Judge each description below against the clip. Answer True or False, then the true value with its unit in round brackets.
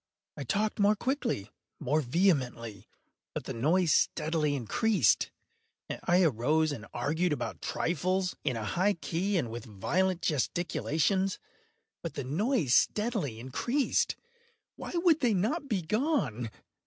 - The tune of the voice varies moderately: False (7.9 semitones)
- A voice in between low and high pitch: True (165 Hz)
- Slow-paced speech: True (125 wpm)